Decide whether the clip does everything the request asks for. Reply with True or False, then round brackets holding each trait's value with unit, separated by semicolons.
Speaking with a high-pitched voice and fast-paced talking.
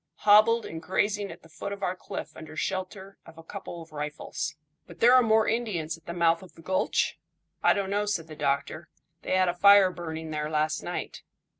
False (180 Hz; 210 wpm)